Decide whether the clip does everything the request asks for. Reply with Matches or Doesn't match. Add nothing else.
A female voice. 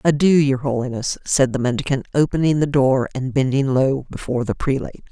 Matches